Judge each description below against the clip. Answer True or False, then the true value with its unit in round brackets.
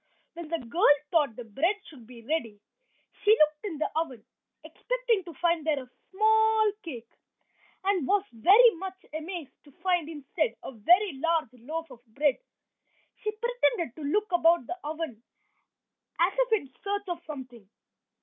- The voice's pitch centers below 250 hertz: False (330 Hz)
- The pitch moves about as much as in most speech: False (6.2 semitones)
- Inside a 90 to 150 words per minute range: False (160 wpm)